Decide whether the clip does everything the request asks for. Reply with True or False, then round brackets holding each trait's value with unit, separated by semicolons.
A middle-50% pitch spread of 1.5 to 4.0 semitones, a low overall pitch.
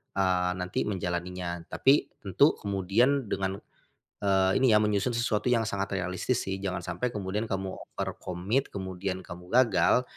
True (2.8 semitones; 95 Hz)